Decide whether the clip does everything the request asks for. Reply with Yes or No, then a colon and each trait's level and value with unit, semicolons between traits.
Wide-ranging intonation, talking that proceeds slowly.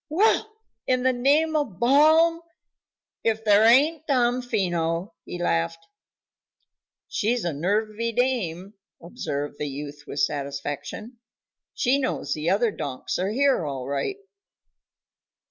Yes: wide, 8.2 semitones; slow, 115 wpm